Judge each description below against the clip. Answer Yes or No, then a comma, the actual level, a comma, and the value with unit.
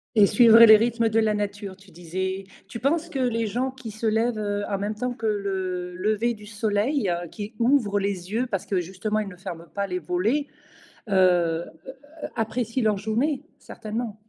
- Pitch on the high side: Yes, high, 210 Hz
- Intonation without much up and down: No, average, 3.1 semitones